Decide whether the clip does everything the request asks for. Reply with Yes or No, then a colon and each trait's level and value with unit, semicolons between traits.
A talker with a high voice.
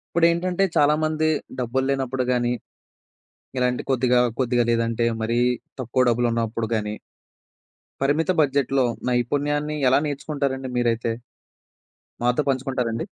No: low, 130 Hz